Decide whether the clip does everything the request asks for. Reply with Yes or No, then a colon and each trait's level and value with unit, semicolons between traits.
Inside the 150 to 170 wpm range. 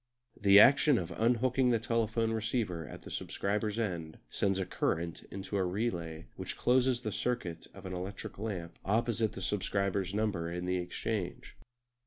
Yes: average, 160 wpm